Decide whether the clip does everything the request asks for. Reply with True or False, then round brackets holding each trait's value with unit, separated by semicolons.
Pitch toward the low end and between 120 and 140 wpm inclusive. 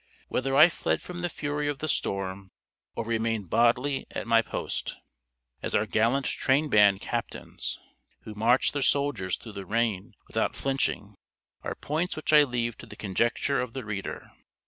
False (120 Hz; 170 wpm)